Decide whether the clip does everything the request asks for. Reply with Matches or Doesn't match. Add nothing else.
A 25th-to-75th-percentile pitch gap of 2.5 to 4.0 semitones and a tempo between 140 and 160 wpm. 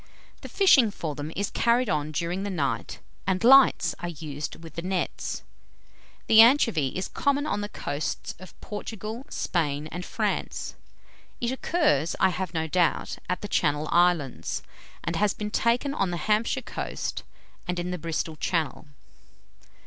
Doesn't match